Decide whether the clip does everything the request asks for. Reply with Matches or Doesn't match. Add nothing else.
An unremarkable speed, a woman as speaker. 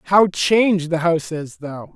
Doesn't match